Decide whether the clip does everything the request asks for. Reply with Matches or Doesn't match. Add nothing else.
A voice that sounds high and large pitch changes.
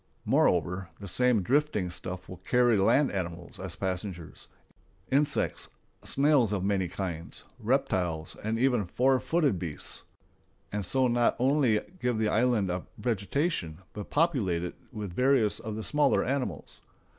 Doesn't match